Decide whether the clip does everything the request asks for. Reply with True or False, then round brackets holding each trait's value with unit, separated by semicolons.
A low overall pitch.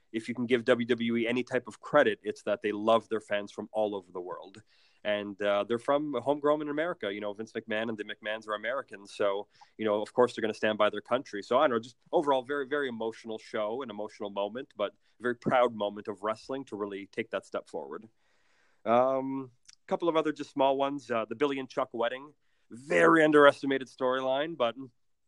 True (120 Hz)